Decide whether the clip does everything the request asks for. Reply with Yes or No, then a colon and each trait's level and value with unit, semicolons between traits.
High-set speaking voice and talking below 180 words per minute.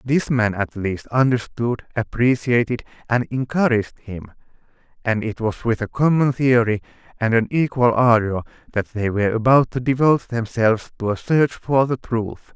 No: low, 120 Hz; average, 160 wpm